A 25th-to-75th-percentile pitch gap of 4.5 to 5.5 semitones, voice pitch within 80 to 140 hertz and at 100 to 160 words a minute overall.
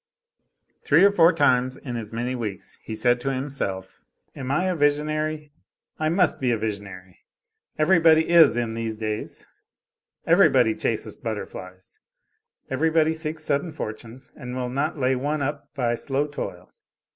Yes: average, 5.0 semitones; low, 135 Hz; average, 145 wpm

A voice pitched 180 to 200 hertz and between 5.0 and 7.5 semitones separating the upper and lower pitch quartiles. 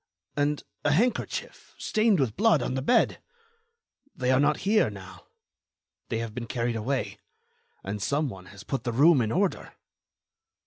No: low, 135 Hz; average, 5.3 semitones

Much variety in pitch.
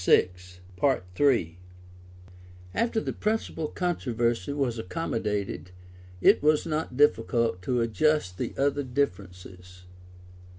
Yes: wide, 7.6 semitones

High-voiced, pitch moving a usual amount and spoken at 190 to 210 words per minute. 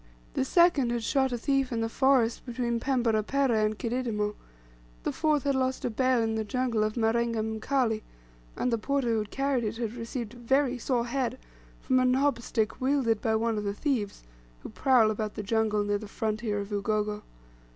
Yes: high, 235 Hz; average, 3.1 semitones; average, 195 wpm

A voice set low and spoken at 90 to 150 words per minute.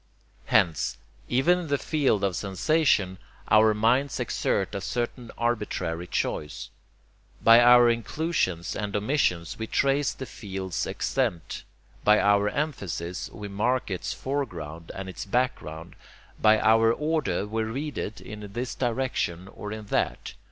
Yes: low, 110 Hz; slow, 135 wpm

